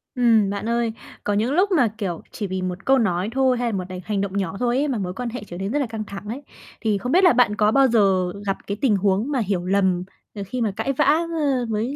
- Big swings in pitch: No, average, 4.4 semitones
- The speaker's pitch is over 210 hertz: Yes, high, 220 Hz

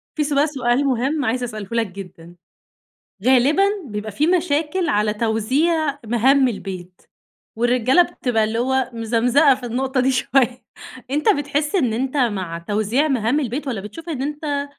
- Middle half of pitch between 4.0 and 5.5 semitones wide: Yes, average, 4.4 semitones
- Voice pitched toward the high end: Yes, very high, 255 Hz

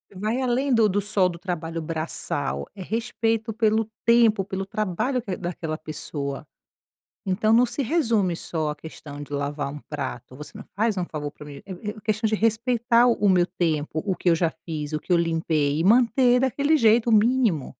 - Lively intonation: Yes, wide, 6.3 semitones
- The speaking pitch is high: Yes, high, 195 Hz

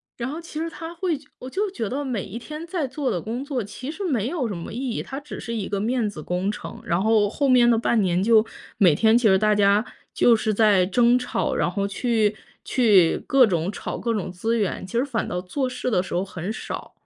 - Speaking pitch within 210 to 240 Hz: Yes, high, 225 Hz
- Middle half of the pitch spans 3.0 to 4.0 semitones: No, average, 4.5 semitones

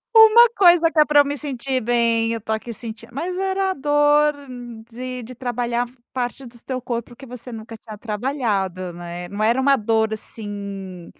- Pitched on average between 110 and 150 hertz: No, high, 240 Hz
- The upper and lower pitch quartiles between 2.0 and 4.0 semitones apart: No, average, 4.5 semitones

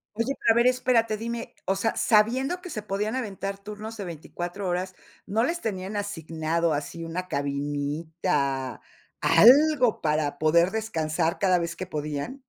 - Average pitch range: No, wide, 5.7 semitones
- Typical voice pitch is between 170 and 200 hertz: Yes, high, 190 Hz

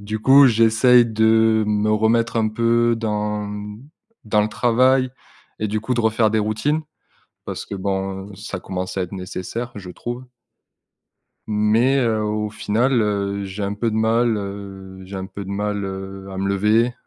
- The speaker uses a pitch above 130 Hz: No, low, 105 Hz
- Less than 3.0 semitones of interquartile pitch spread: Yes, narrow, 2.5 semitones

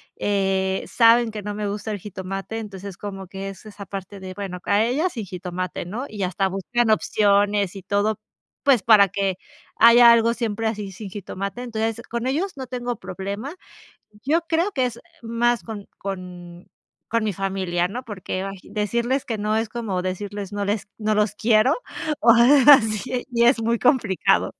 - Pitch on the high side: Yes, high, 210 Hz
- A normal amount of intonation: Yes, average, 3.2 semitones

